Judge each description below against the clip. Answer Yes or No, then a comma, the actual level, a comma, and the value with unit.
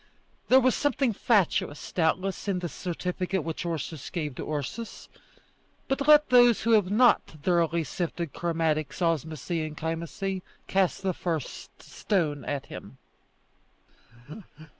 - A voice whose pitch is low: No, medium, 175 Hz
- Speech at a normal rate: No, slow, 125 wpm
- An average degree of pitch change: Yes, average, 4.1 semitones